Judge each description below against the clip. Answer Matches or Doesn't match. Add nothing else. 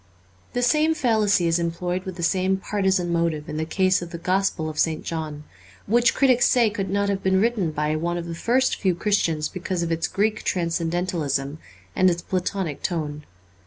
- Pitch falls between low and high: Matches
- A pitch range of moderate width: Matches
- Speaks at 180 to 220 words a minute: Matches